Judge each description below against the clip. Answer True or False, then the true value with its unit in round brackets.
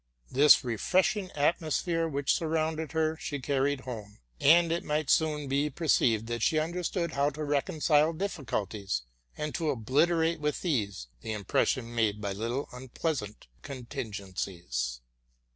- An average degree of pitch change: False (6.0 semitones)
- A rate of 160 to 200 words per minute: False (145 wpm)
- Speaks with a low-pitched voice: False (145 Hz)